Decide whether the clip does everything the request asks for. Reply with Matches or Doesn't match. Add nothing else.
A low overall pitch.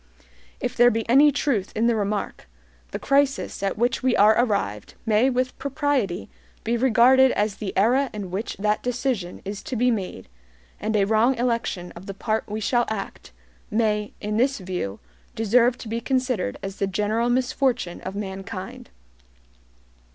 Doesn't match